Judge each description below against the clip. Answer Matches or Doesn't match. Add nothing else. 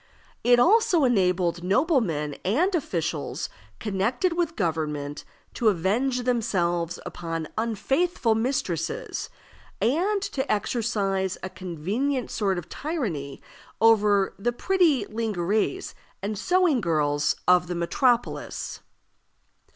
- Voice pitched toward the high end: Matches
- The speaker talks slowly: Matches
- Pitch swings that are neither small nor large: Doesn't match